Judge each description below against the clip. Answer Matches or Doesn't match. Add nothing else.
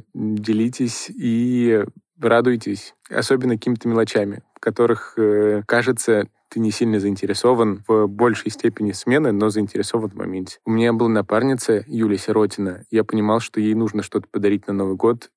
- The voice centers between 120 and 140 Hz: Doesn't match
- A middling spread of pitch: Doesn't match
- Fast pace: Doesn't match